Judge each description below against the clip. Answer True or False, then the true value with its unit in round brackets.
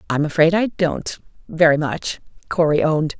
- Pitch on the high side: False (160 Hz)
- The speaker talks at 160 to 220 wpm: False (150 wpm)